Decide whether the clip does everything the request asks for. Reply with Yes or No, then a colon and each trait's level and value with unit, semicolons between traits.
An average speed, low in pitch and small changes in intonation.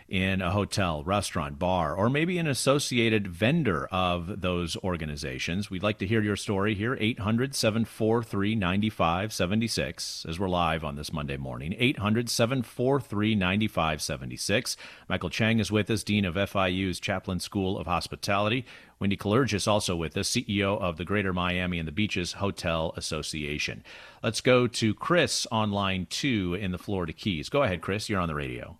No: average, 165 wpm; low, 100 Hz; average, 3.8 semitones